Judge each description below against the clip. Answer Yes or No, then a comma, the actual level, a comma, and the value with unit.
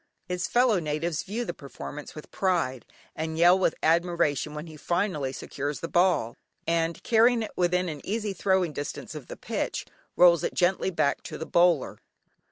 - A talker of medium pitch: Yes, medium, 170 Hz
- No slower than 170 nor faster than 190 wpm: Yes, average, 175 wpm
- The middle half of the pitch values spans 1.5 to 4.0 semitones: Yes, average, 3.6 semitones